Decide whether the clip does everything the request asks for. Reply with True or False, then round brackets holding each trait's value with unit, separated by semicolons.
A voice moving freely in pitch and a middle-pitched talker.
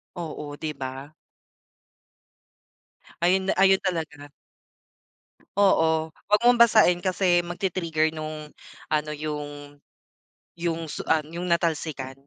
False (2.9 semitones; 160 Hz)